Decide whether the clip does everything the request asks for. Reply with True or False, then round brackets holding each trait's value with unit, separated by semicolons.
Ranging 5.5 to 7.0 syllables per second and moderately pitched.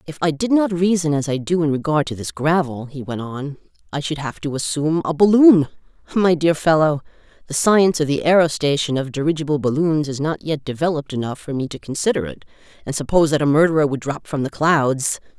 True (5.9 syllables/s; 155 Hz)